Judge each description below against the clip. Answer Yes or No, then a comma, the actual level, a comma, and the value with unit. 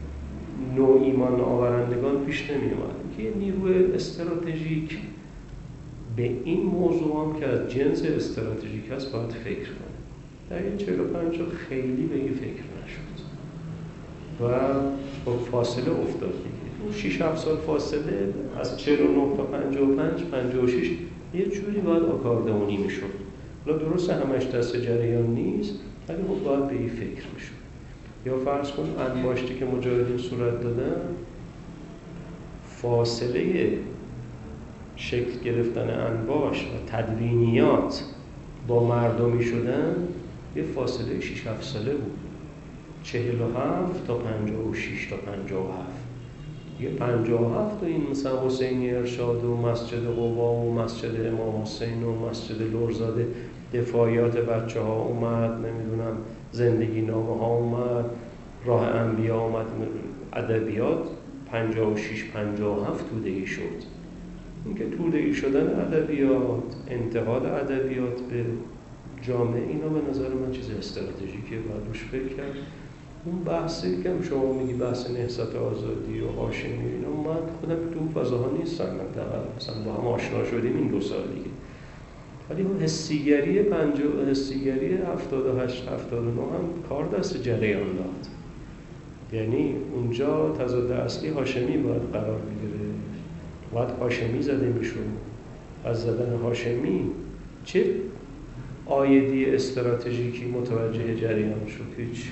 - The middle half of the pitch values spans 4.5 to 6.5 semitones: No, average, 3.4 semitones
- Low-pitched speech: Yes, low, 125 Hz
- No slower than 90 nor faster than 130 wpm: Yes, average, 125 wpm